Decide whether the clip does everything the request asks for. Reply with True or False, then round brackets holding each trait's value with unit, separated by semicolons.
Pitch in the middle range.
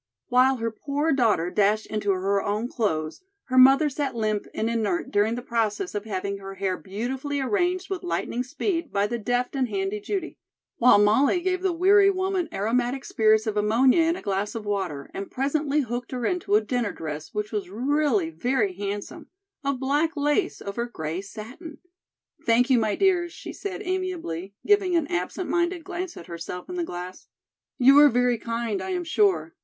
False (245 Hz)